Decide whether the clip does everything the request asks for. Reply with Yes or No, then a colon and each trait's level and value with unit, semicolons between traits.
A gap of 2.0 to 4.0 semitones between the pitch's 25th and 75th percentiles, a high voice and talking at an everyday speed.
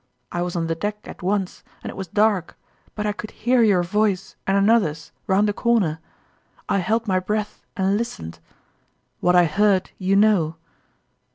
Yes: average, 3.0 semitones; high, 195 Hz; average, 175 wpm